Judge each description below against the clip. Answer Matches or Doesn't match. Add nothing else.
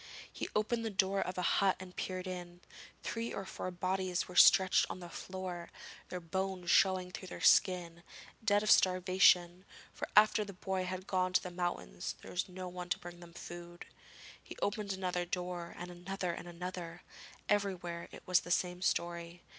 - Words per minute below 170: Doesn't match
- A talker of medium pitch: Matches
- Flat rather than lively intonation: Matches